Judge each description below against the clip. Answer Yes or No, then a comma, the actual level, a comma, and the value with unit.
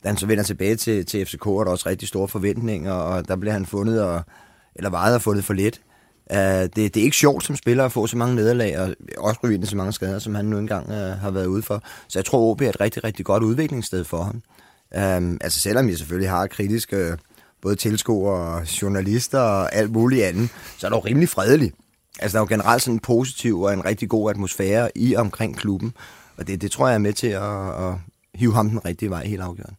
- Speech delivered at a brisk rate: Yes, fast, 245 wpm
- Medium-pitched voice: No, low, 105 Hz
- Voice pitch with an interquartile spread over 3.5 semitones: No, average, 2.8 semitones